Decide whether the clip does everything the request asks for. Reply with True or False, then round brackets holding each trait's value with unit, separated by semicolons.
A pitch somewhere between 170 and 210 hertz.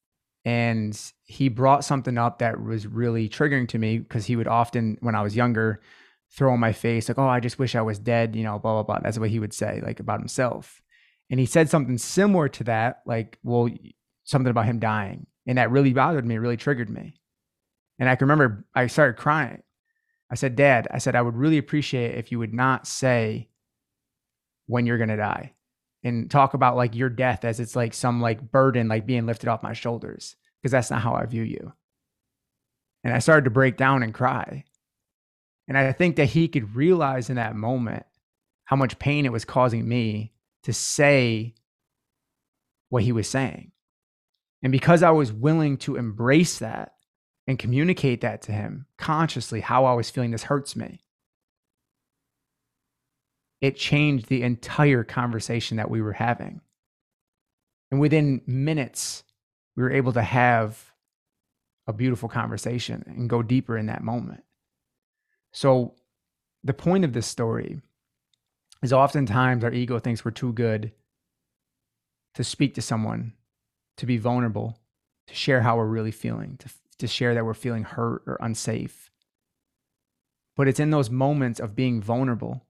False (120 Hz)